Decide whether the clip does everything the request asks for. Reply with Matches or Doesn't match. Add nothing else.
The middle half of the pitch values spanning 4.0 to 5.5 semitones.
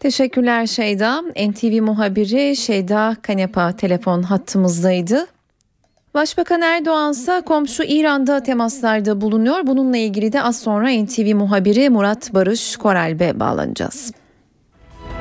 Matches